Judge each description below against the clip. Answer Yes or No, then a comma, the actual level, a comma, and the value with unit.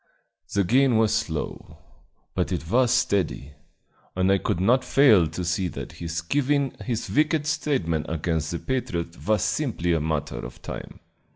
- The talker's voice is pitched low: Yes, very low, 95 Hz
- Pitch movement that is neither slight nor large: No, wide, 7.6 semitones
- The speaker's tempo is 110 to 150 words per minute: No, average, 160 wpm